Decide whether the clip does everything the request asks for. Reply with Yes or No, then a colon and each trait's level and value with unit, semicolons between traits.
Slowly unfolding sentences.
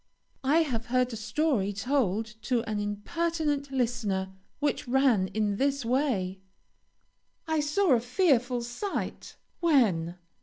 Yes: slow, 125 wpm